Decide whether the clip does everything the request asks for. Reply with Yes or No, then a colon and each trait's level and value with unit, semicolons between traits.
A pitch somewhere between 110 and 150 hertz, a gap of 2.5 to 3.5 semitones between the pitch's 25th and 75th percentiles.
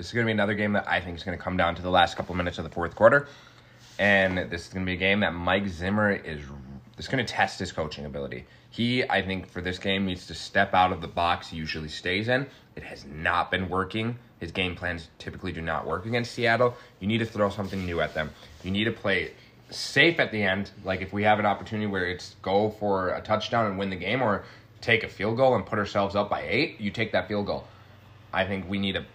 No: low, 100 Hz; average, 3.1 semitones